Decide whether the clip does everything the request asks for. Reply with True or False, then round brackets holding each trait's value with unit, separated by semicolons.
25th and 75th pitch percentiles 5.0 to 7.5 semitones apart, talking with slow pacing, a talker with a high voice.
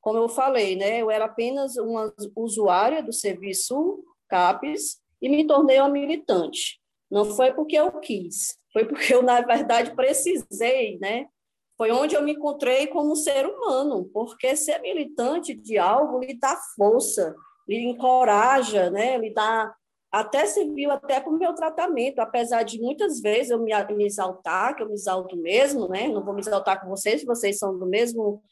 False (5.3 semitones; 170 wpm; 240 Hz)